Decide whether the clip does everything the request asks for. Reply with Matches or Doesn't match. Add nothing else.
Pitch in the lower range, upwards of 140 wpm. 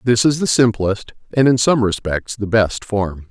Matches